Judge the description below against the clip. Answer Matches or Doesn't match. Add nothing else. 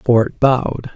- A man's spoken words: Matches